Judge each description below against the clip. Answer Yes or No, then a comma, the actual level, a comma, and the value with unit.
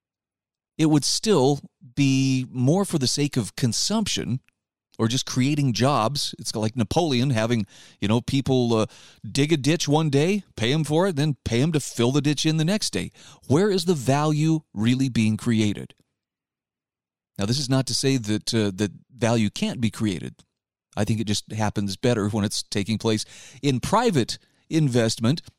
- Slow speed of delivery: No, average, 175 wpm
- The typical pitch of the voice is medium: No, low, 130 Hz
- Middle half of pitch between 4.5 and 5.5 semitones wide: Yes, average, 5.2 semitones